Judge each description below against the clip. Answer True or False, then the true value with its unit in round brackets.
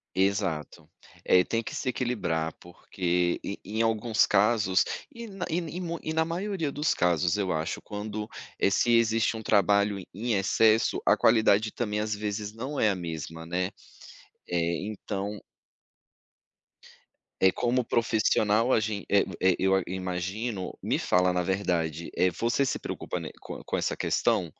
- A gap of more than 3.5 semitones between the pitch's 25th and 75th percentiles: True (3.9 semitones)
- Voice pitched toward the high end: False (105 Hz)